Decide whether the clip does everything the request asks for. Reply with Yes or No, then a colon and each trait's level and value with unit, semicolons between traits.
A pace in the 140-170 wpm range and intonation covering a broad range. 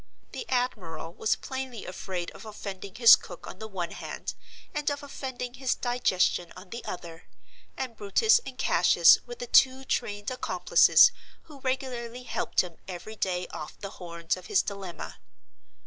Yes: average, 155 wpm; wide, 5.9 semitones